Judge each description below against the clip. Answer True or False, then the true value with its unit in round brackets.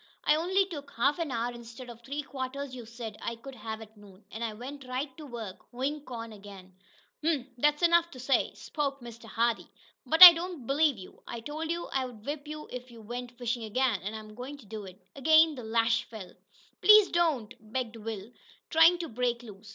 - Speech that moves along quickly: True (210 wpm)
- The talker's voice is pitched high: True (250 Hz)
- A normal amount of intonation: True (4.7 semitones)